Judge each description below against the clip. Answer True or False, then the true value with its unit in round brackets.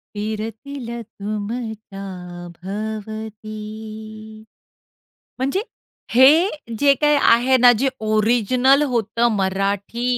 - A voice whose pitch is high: True (220 Hz)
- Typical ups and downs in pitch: True (3.0 semitones)